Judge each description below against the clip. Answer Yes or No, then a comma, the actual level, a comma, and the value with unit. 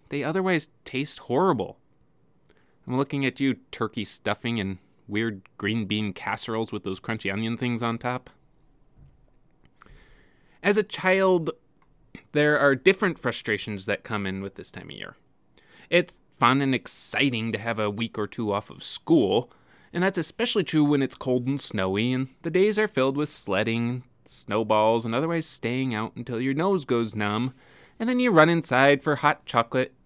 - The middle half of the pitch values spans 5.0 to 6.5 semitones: Yes, wide, 5.4 semitones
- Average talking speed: Yes, average, 170 wpm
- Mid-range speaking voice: No, low, 125 Hz